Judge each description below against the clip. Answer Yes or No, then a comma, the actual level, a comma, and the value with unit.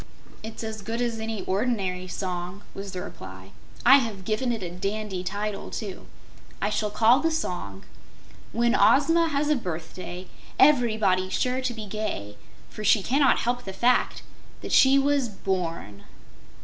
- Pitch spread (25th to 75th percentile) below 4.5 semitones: No, average, 4.9 semitones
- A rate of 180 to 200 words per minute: No, average, 155 wpm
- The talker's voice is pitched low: No, high, 215 Hz